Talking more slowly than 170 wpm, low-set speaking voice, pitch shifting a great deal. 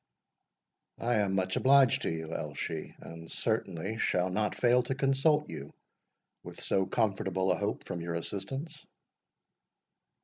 Yes: slow, 135 wpm; low, 100 Hz; wide, 6.7 semitones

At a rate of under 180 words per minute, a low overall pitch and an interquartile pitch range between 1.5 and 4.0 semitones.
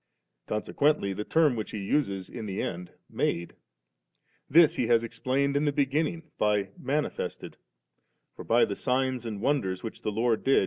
No: average, 165 wpm; low, 120 Hz; average, 5.2 semitones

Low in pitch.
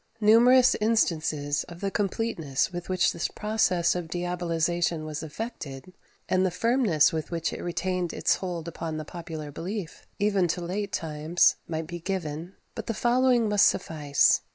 No: medium, 175 Hz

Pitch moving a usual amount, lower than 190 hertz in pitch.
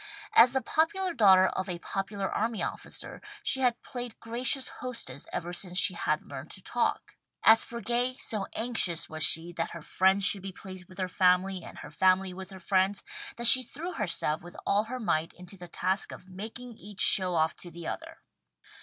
No: average, 4.5 semitones; high, 195 Hz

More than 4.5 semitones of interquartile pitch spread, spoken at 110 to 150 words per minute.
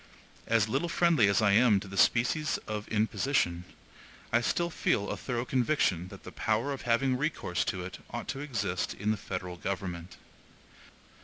No: average, 5.2 semitones; average, 170 wpm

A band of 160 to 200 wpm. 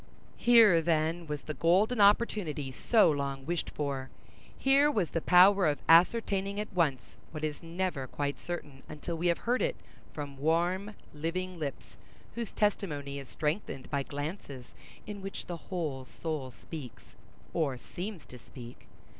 No: average, 145 wpm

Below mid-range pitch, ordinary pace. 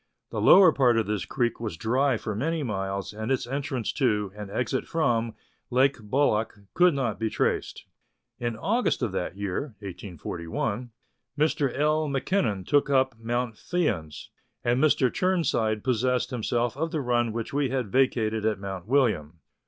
Yes: low, 120 Hz; average, 160 wpm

